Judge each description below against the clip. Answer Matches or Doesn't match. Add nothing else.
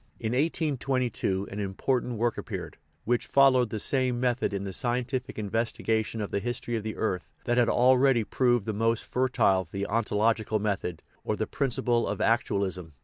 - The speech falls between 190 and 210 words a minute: Doesn't match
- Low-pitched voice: Matches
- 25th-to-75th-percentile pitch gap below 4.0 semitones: Matches